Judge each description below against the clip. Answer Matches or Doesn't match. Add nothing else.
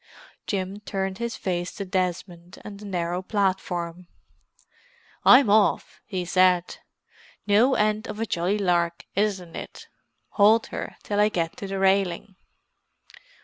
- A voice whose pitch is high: Matches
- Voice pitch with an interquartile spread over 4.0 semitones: Doesn't match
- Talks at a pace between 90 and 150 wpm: Matches